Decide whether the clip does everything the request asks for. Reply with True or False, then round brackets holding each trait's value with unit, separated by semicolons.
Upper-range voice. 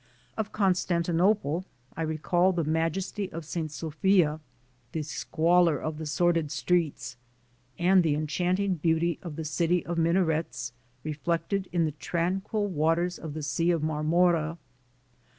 False (165 Hz)